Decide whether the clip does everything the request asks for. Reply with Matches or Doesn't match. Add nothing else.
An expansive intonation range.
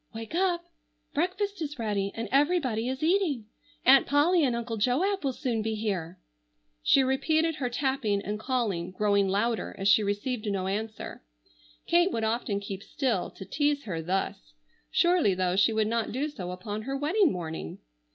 Matches